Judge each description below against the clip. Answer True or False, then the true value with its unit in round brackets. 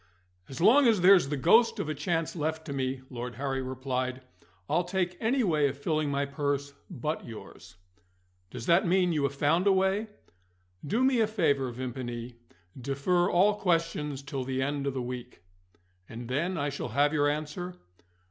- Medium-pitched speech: True (145 Hz)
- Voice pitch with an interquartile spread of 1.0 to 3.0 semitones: False (5.1 semitones)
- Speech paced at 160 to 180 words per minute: True (175 wpm)